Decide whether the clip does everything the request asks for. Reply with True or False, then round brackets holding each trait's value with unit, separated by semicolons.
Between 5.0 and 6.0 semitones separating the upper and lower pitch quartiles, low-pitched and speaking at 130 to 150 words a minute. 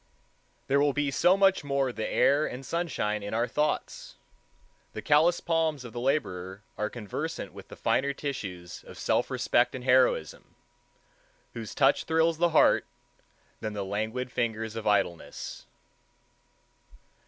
True (5.5 semitones; 125 Hz; 140 wpm)